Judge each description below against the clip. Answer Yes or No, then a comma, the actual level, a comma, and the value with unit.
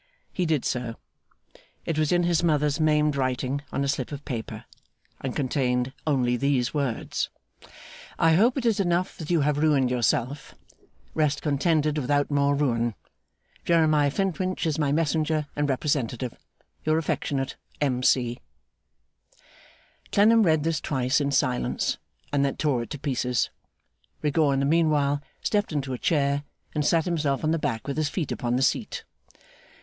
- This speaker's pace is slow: No, average, 155 wpm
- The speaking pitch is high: No, medium, 145 Hz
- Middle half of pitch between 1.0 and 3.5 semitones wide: Yes, average, 3.0 semitones